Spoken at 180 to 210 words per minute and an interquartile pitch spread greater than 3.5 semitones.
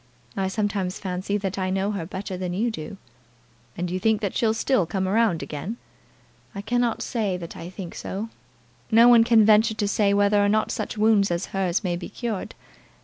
No: average, 200 wpm; average, 2.8 semitones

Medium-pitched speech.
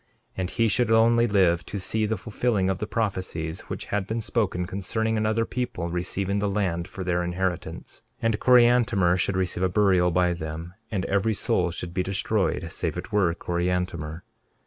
No: very low, 95 Hz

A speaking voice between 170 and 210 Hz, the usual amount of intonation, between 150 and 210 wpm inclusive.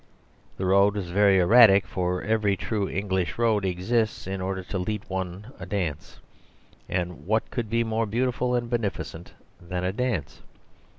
No: low, 100 Hz; average, 3.3 semitones; average, 160 wpm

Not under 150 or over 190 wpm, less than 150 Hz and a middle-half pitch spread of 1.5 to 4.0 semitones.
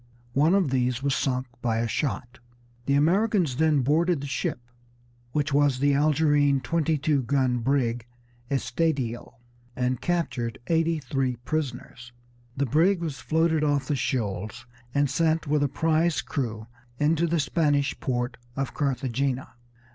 No: average, 140 wpm; medium, 140 Hz; average, 3.7 semitones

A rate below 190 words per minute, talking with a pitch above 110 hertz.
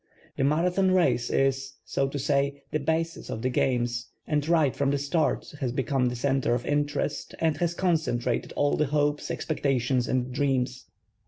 Yes: average, 170 wpm; medium, 140 Hz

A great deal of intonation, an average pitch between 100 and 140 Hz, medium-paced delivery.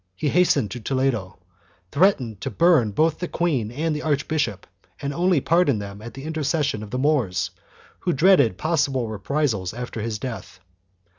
Yes: wide, 6.4 semitones; low, 135 Hz; average, 165 wpm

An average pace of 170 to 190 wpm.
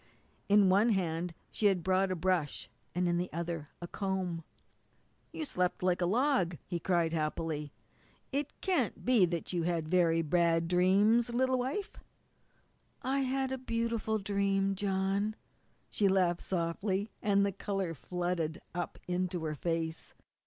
No: average, 145 wpm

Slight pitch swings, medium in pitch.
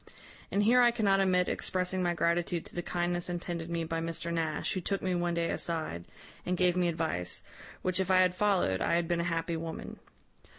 Yes: narrow, 1.7 semitones; medium, 175 Hz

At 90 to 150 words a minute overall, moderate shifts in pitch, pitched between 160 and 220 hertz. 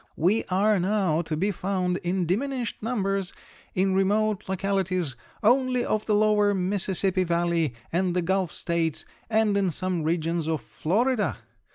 Yes: average, 145 wpm; average, 3.1 semitones; high, 190 Hz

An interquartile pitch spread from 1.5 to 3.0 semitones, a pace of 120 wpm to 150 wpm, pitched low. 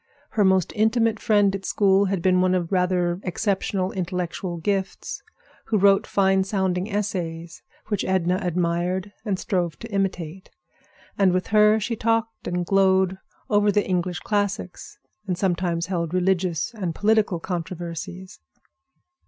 No: narrow, 2.4 semitones; slow, 135 wpm; high, 190 Hz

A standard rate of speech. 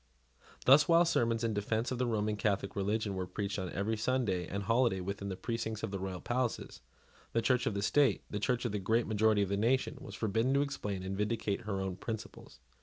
No: fast, 220 wpm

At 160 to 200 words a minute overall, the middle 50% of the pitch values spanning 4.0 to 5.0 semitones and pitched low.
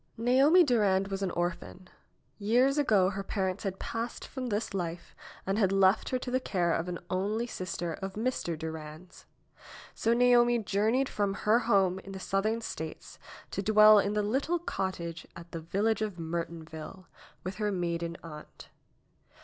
No: average, 170 wpm; average, 4.3 semitones; high, 195 Hz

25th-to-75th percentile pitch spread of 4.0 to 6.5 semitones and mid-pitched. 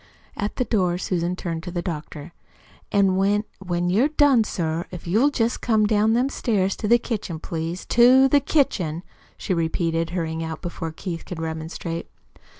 Yes: average, 4.9 semitones; medium, 180 Hz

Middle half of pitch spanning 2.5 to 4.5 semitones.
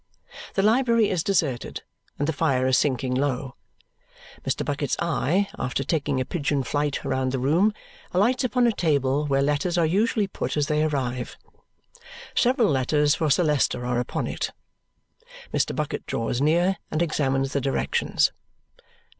No: average, 4.9 semitones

